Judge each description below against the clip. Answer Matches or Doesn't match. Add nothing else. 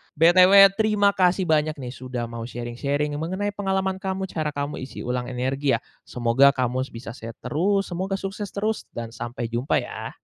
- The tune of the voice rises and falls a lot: Matches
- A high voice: Doesn't match